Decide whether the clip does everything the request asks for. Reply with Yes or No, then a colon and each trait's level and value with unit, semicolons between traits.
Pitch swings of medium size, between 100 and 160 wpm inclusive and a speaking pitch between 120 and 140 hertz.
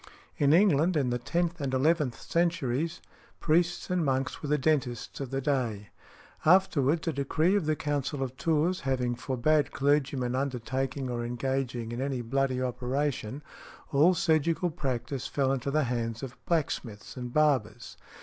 Yes: average, 3.6 semitones; average, 150 wpm; low, 135 Hz